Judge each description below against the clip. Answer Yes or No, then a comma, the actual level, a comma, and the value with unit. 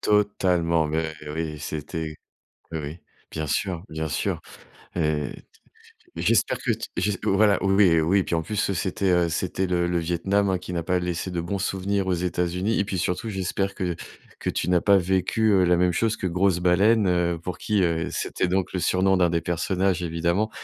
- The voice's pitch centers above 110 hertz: No, very low, 90 Hz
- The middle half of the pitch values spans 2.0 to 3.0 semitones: Yes, narrow, 2.4 semitones